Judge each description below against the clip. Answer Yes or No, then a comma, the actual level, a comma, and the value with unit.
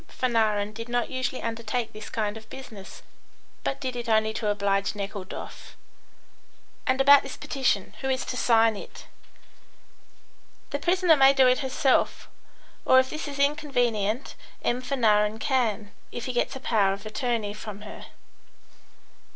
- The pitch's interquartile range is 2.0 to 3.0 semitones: No, average, 3.8 semitones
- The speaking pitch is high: Yes, high, 235 Hz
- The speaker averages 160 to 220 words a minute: No, average, 150 wpm